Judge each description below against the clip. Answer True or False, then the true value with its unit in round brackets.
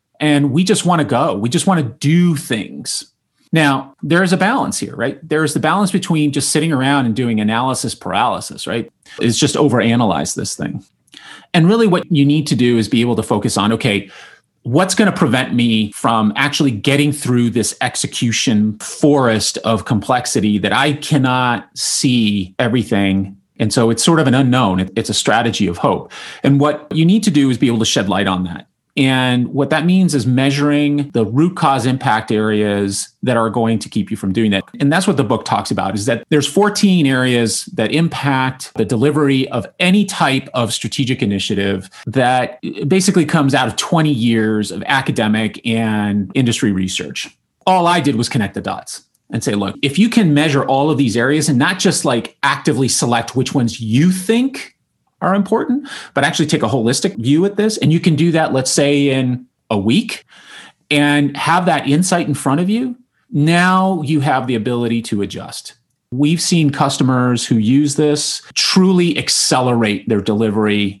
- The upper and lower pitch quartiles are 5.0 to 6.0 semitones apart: True (5.4 semitones)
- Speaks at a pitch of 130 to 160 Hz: True (135 Hz)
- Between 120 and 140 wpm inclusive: False (190 wpm)